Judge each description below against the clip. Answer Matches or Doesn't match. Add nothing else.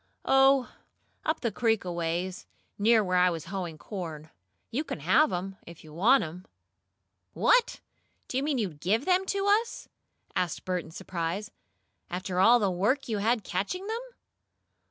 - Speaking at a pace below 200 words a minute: Matches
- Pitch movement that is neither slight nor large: Doesn't match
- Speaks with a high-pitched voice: Matches